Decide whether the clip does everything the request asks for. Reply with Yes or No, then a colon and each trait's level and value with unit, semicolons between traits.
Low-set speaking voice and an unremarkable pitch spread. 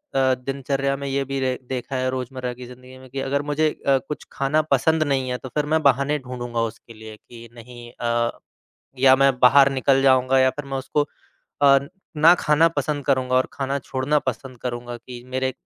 No: low, 130 Hz; narrow, 1.7 semitones